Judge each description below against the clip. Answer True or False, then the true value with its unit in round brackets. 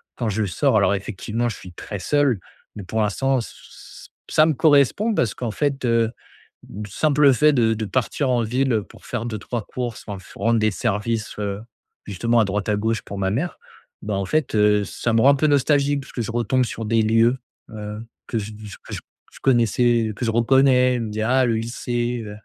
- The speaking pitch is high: False (115 Hz)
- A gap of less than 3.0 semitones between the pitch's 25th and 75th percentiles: False (3.3 semitones)